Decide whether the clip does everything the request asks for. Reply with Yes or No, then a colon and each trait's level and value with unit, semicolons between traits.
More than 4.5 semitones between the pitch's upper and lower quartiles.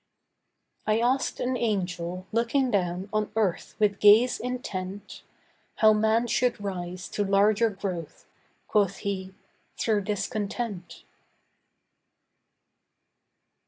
No: average, 3.2 semitones